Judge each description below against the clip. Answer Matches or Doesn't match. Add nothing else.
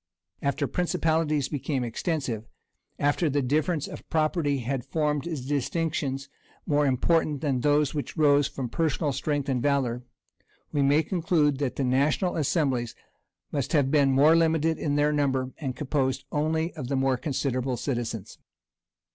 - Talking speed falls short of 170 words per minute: Matches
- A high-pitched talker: Doesn't match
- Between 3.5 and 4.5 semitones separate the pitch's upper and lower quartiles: Doesn't match